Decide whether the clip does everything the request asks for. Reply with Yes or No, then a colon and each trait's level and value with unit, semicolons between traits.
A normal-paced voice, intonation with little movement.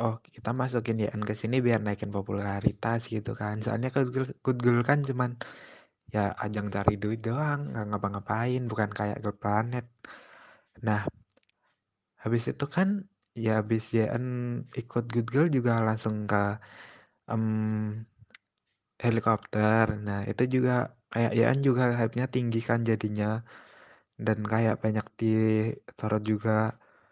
Yes: average, 130 wpm; narrow, 2.3 semitones